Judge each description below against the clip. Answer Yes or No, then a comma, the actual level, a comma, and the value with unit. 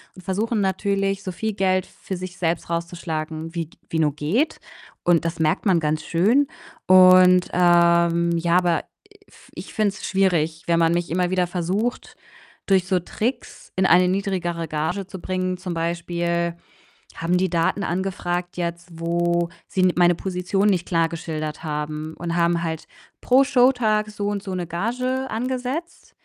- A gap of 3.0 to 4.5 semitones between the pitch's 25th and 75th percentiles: No, narrow, 2.5 semitones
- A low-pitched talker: No, medium, 180 Hz